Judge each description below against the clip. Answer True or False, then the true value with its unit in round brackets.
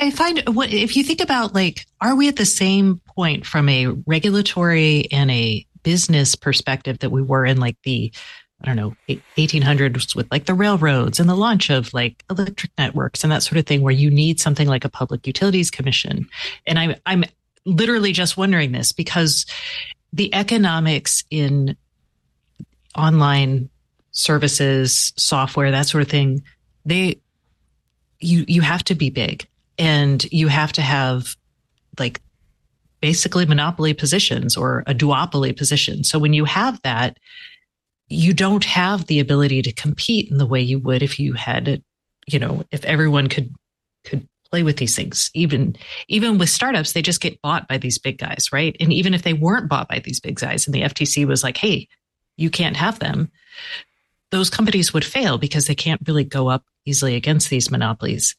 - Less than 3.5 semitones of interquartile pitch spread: False (4.5 semitones)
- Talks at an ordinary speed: True (175 wpm)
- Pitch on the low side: False (155 Hz)